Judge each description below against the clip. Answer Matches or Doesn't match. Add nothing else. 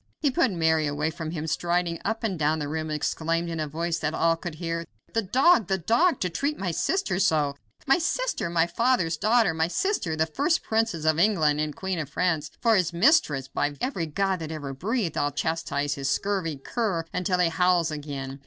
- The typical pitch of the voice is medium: Matches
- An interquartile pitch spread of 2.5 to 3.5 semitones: Doesn't match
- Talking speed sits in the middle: Doesn't match